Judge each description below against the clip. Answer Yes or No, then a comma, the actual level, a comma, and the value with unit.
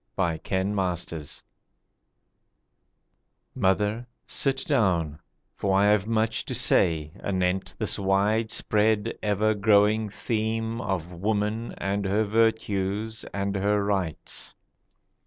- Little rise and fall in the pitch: Yes, narrow, 2.3 semitones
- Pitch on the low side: Yes, low, 105 Hz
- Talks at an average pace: No, slow, 100 wpm